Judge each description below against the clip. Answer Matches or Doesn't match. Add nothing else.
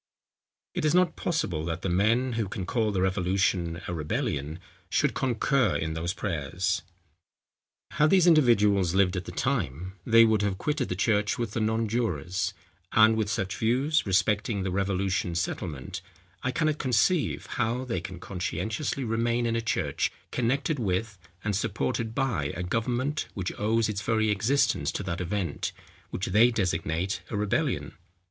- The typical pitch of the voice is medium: Doesn't match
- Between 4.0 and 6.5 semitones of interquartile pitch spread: Matches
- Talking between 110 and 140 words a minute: Doesn't match